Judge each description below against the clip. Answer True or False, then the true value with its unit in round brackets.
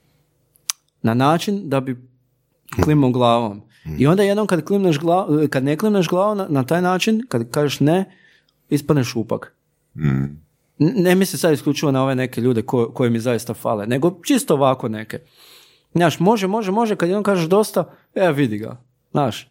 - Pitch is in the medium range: True (150 Hz)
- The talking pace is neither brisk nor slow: False (165 wpm)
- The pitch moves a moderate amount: False (6.2 semitones)